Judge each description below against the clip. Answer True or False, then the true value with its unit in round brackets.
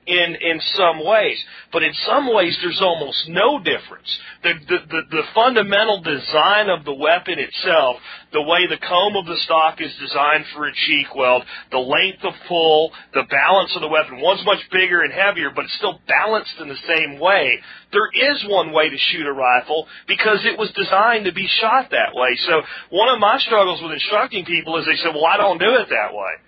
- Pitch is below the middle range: False (170 Hz)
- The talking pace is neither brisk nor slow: False (210 wpm)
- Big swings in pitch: False (4.2 semitones)